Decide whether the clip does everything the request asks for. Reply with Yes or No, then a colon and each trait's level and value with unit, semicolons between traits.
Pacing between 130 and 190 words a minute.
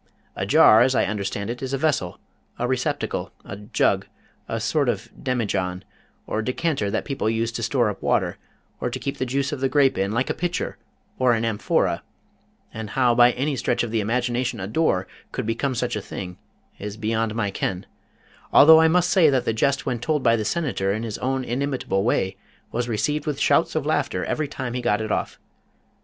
No: fast, 205 wpm